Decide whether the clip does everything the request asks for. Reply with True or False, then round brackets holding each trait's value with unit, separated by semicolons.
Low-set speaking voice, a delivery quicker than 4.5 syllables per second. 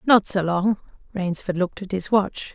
False (190 Hz; 4.8 syllables/s)